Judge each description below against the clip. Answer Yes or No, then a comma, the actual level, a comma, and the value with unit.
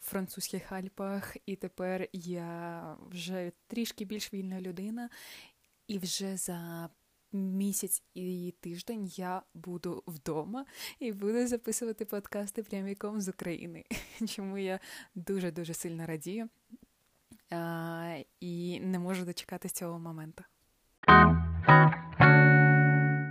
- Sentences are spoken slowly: Yes, slow, 100 wpm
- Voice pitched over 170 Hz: Yes, medium, 185 Hz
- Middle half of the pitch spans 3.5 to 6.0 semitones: No, average, 2.8 semitones